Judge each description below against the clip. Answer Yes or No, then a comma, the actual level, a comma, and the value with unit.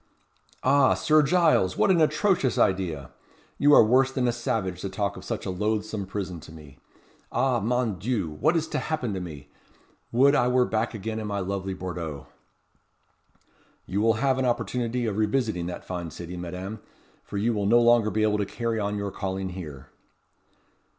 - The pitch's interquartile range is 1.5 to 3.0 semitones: No, average, 4.9 semitones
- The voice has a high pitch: No, low, 105 Hz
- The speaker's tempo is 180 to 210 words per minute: Yes, average, 185 wpm